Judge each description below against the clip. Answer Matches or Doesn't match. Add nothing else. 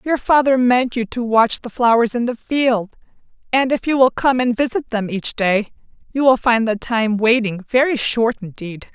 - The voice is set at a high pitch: Matches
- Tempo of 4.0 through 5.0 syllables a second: Matches